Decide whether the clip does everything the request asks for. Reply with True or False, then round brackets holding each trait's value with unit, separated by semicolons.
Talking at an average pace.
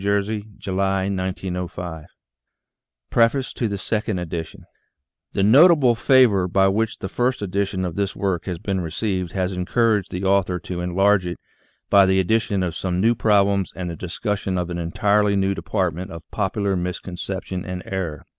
True (155 wpm)